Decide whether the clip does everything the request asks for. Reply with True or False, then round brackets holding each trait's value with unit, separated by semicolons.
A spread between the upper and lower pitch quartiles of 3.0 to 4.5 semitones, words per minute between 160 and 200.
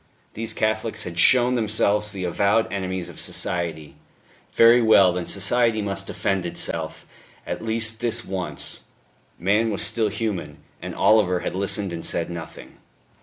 False (3.5 semitones; 145 wpm)